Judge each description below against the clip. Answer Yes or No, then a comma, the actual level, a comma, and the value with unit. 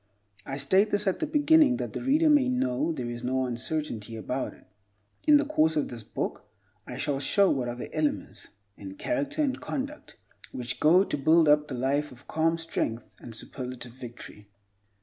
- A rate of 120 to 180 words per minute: No, average, 190 wpm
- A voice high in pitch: No, medium, 150 Hz